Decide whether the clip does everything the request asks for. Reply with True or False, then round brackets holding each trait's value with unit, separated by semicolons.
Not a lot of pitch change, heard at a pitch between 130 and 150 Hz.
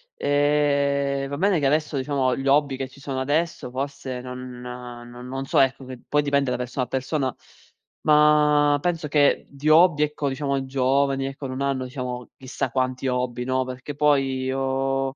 True (2.0 semitones; 135 Hz)